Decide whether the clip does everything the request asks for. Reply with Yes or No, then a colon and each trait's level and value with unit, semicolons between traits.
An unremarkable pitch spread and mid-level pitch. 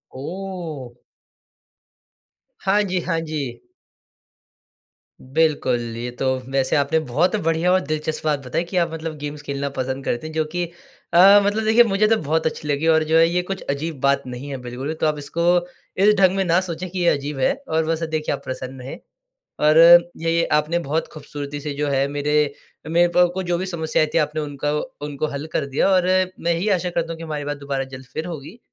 Yes: average, 3.5 semitones; medium, 155 Hz